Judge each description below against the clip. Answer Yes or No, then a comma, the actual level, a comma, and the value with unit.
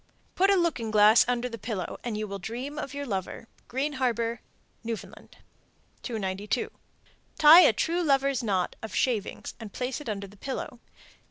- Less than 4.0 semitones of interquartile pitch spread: No, average, 4.7 semitones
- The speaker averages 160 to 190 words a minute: Yes, average, 165 wpm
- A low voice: No, high, 235 Hz